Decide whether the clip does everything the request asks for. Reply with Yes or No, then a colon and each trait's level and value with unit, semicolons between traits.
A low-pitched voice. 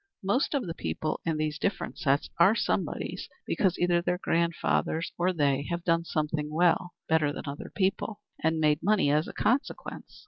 No: medium, 165 Hz